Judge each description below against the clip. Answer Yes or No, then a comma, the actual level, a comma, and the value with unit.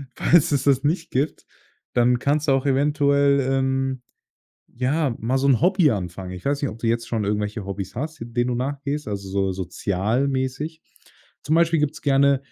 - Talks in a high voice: No, low, 135 Hz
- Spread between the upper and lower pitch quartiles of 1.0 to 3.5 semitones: No, average, 4.0 semitones